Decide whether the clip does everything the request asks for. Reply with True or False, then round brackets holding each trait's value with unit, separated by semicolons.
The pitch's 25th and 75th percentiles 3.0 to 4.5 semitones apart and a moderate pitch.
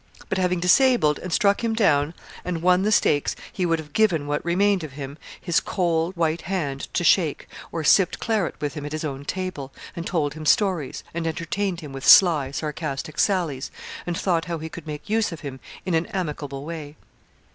True (3.7 semitones; 165 Hz)